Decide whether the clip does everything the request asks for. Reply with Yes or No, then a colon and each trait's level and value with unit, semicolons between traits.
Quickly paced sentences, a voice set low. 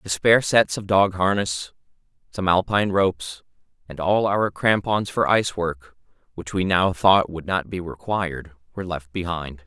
No: average, 170 wpm; very low, 90 Hz